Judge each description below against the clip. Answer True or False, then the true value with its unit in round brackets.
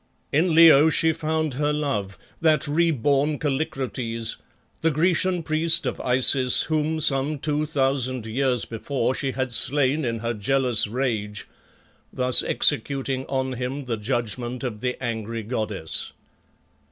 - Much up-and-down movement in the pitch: False (4.1 semitones)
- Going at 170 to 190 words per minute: False (135 wpm)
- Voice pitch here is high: False (135 Hz)